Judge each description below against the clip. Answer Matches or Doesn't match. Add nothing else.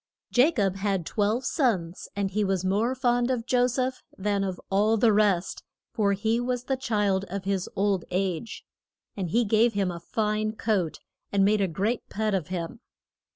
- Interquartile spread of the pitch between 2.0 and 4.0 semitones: Matches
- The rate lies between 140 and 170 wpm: Doesn't match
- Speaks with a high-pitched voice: Matches